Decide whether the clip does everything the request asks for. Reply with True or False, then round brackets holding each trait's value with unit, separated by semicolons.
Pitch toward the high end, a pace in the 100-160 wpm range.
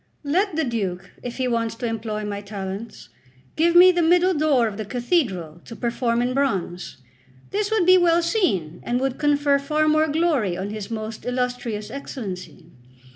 False (245 Hz; 175 wpm)